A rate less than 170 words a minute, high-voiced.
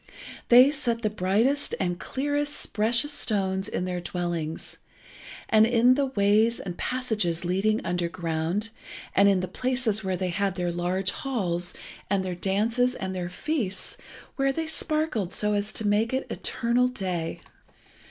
Yes: average, 150 wpm; high, 205 Hz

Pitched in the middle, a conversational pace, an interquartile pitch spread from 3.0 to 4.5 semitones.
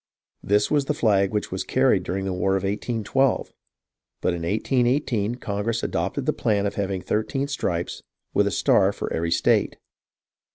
No: low, 105 Hz; average, 180 wpm; average, 3.8 semitones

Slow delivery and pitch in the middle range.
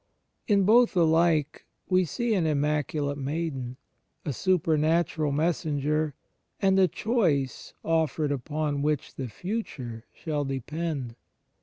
Yes: slow, 110 wpm; medium, 155 Hz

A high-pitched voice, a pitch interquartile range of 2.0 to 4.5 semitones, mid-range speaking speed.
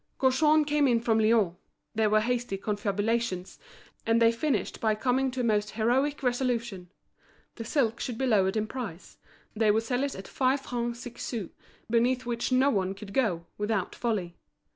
Yes: high, 230 Hz; average, 3.2 semitones; average, 175 wpm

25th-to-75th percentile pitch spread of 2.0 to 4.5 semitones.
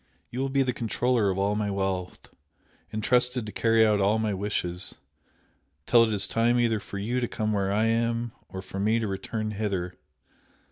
Yes: average, 2.7 semitones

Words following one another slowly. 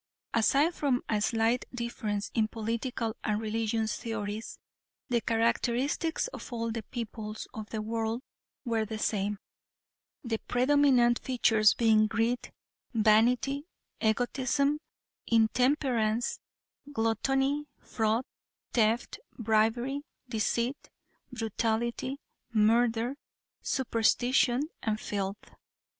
Yes: slow, 90 wpm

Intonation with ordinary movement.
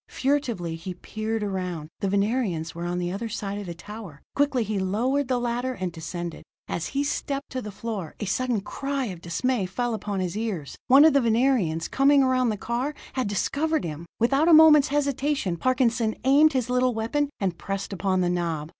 No: wide, 6.1 semitones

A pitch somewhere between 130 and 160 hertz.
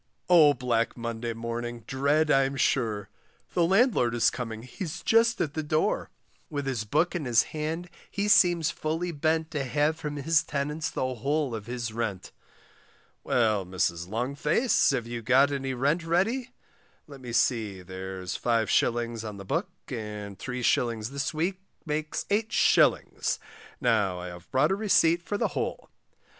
Yes: low, 135 Hz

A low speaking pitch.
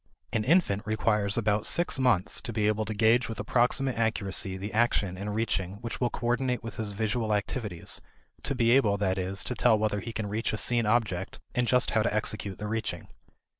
Yes: low, 110 Hz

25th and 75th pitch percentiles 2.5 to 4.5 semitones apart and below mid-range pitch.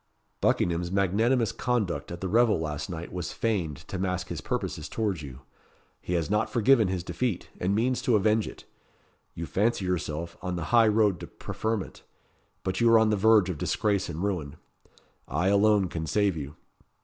Yes: average, 4.2 semitones; very low, 95 Hz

